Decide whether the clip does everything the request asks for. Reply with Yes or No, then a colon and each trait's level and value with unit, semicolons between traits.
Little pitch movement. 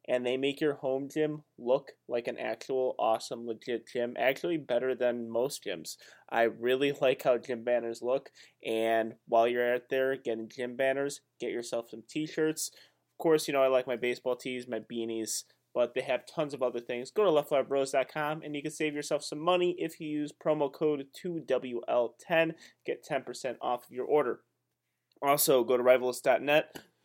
No: average, 3.6 semitones